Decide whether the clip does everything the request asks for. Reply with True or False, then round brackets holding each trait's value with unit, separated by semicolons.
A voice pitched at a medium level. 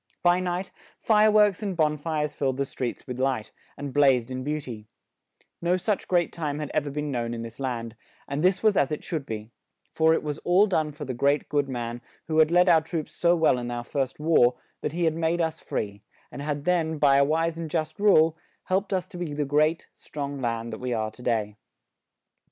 True (150 Hz)